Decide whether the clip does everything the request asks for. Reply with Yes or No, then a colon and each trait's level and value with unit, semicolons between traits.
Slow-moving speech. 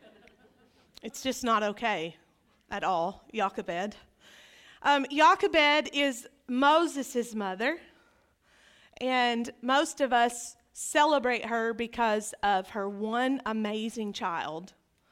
Yes: slow, 95 wpm